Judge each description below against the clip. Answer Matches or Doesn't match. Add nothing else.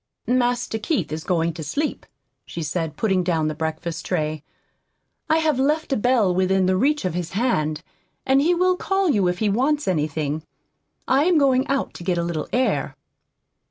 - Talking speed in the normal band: Matches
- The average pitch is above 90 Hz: Matches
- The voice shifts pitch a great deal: Matches